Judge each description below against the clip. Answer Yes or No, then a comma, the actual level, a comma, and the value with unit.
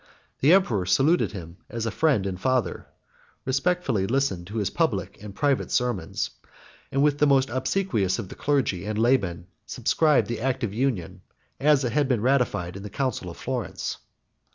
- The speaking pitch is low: Yes, low, 125 Hz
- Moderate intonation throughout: No, wide, 5.8 semitones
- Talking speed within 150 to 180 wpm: Yes, average, 175 wpm